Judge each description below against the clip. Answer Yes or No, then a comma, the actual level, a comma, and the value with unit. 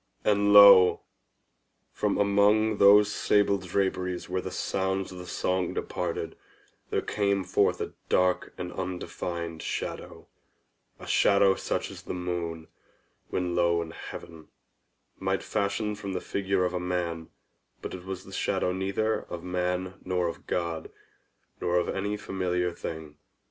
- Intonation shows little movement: Yes, narrow, 2.0 semitones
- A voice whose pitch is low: Yes, very low, 90 Hz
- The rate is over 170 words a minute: No, average, 140 wpm